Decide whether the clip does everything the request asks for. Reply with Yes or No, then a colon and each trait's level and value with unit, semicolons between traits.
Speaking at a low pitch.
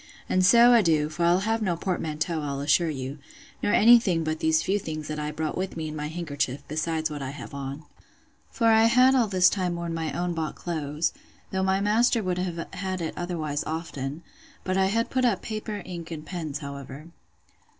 No: medium, 170 Hz